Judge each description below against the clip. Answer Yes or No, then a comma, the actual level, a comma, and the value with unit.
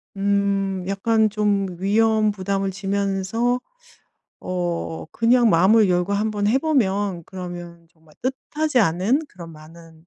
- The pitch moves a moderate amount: Yes, average, 3.5 semitones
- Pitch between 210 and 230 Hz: No, high, 195 Hz